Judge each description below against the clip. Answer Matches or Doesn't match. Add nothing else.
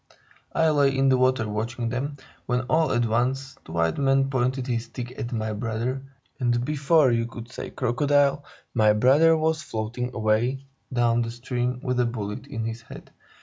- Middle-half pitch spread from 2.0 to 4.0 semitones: Matches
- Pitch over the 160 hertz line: Doesn't match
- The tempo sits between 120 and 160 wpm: Doesn't match